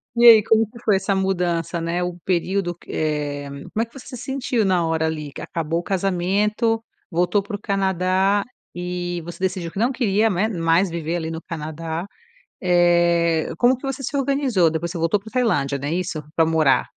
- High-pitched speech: No, medium, 180 Hz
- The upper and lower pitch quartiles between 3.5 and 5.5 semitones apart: Yes, average, 3.9 semitones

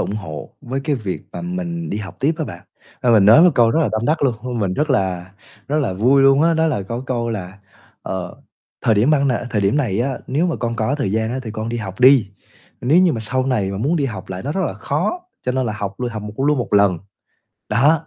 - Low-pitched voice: Yes, low, 120 Hz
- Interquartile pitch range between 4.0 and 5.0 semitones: No, wide, 5.4 semitones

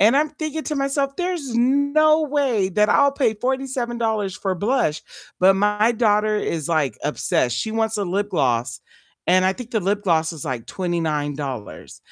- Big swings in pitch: Yes, wide, 7.7 semitones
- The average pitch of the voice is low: No, high, 210 Hz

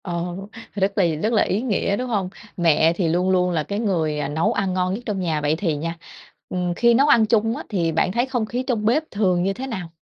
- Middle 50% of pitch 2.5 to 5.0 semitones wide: Yes, average, 4.5 semitones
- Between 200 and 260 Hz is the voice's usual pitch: No, high, 190 Hz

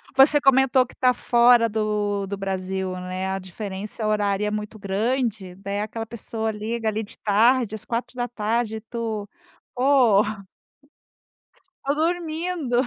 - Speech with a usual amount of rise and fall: Yes, average, 3.3 semitones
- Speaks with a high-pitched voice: Yes, high, 220 Hz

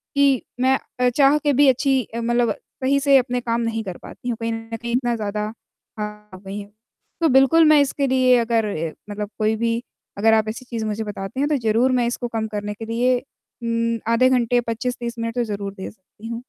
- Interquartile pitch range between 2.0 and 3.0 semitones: Yes, average, 2.7 semitones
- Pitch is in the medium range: No, high, 235 Hz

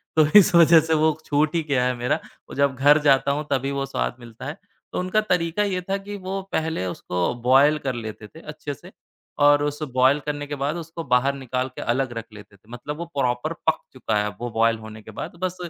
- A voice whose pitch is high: No, medium, 140 Hz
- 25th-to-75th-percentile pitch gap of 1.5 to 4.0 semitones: No, average, 4.4 semitones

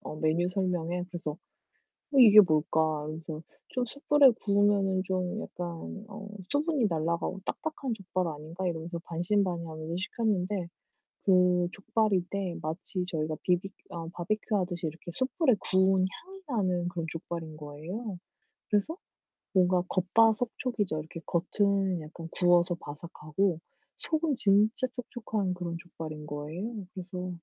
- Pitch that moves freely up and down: No, average, 3.7 semitones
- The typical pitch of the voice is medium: Yes, medium, 180 Hz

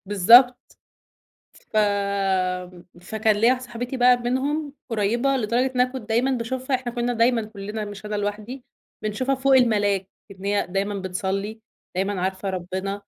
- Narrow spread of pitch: No, average, 3.7 semitones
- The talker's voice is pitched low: No, high, 220 Hz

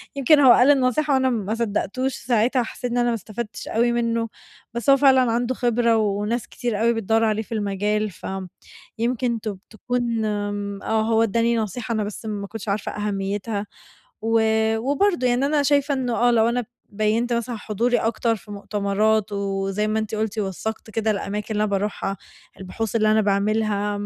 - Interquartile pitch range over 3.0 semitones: No, narrow, 2.5 semitones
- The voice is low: No, high, 220 Hz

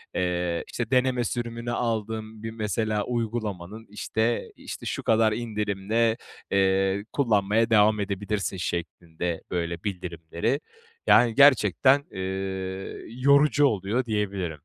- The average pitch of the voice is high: No, low, 105 Hz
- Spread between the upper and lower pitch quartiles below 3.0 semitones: No, average, 3.5 semitones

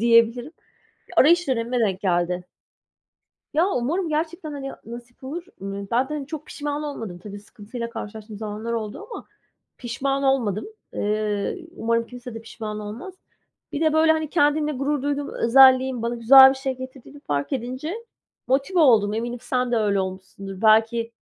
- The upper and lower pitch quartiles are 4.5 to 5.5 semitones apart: Yes, average, 4.8 semitones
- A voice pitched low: No, high, 245 Hz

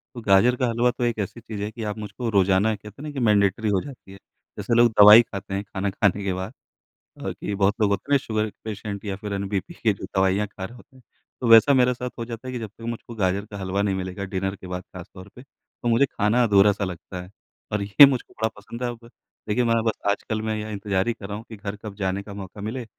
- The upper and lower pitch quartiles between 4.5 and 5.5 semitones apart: No, average, 2.9 semitones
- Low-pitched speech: Yes, low, 105 Hz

